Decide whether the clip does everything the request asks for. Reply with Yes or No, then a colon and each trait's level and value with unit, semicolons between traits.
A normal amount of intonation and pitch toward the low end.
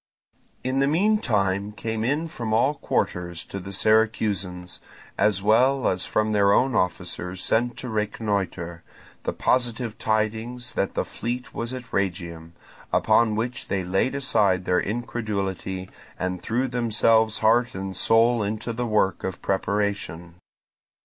Yes: average, 3.8 semitones; low, 110 Hz